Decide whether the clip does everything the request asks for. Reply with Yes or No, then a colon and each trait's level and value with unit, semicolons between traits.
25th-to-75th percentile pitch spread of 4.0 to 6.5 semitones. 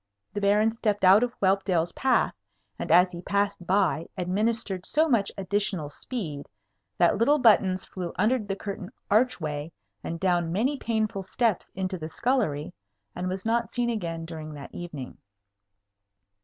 Yes: average, 4.3 semitones